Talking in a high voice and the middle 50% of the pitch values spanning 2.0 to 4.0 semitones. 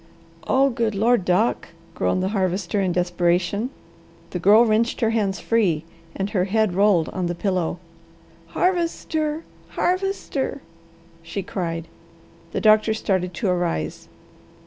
No: high, 200 Hz; average, 4.4 semitones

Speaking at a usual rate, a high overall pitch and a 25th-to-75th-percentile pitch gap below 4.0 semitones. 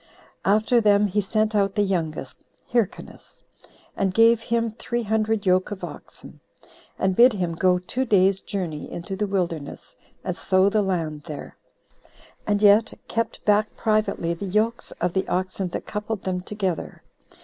Yes: average, 155 wpm; high, 200 Hz; average, 2.8 semitones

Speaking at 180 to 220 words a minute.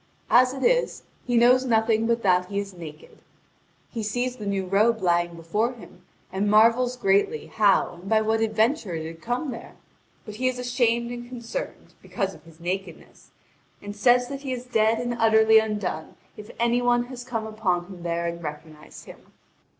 Yes: average, 185 wpm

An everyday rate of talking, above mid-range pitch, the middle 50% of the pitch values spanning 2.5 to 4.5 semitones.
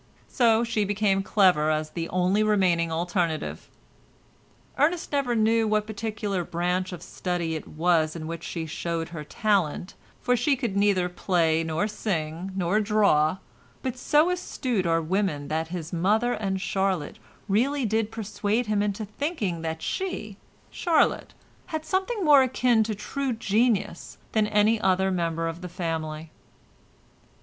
No: average, 145 wpm; high, 195 Hz; average, 4.9 semitones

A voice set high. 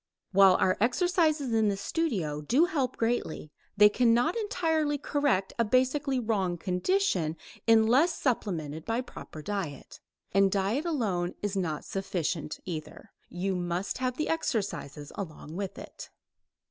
Yes: high, 210 Hz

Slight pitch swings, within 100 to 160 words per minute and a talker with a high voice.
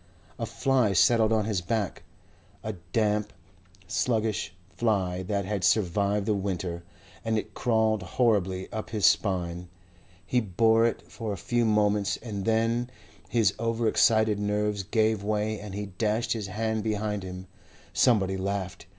No: narrow, 2.3 semitones; average, 145 wpm; low, 105 Hz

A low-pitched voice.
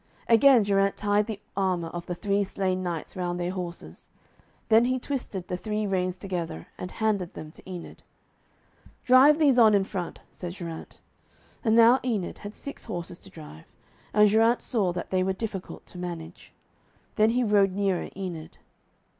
No: high, 195 Hz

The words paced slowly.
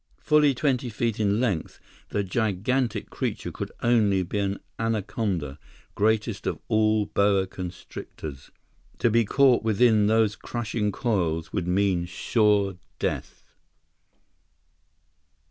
Yes: slow, 110 wpm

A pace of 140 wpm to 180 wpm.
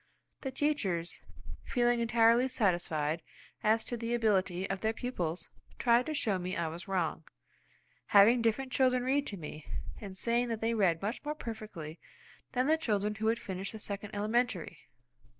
Yes: average, 165 wpm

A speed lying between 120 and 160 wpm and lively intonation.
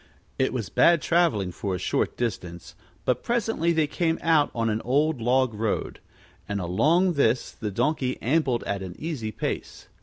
No: average, 170 wpm; wide, 6.8 semitones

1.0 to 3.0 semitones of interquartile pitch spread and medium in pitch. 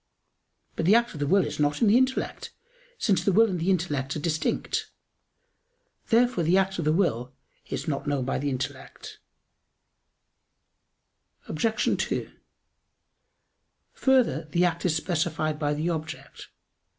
No: average, 4.6 semitones; medium, 165 Hz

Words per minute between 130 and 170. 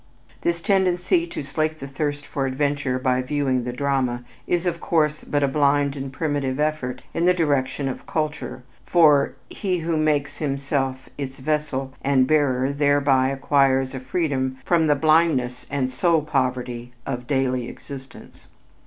Yes: average, 155 wpm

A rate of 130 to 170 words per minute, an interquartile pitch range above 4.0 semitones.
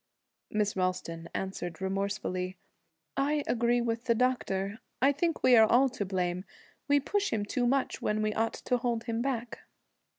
Yes: average, 165 wpm; average, 4.6 semitones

